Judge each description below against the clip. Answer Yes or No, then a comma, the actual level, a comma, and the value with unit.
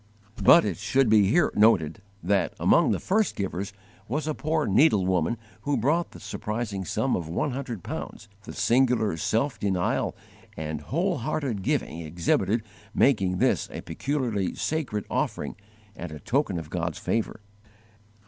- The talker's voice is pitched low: Yes, low, 105 Hz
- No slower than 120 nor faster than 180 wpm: Yes, average, 150 wpm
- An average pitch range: No, wide, 7.1 semitones